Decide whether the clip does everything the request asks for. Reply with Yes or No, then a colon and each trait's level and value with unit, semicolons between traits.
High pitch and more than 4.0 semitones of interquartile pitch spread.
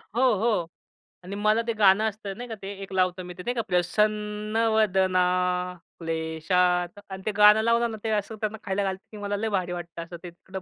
No: high, 195 Hz; average, 3.1 semitones